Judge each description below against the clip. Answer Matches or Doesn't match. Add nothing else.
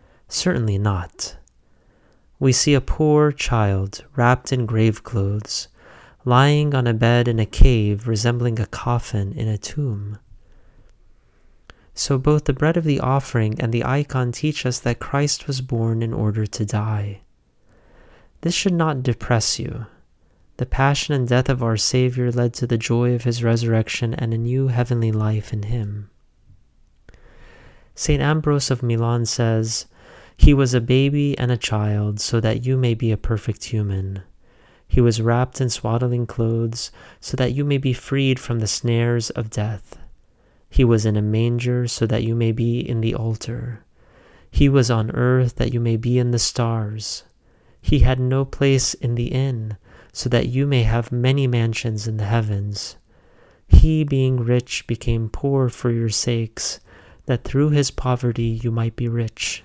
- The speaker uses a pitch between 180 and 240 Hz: Doesn't match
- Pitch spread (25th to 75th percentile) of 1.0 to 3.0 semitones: Matches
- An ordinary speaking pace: Matches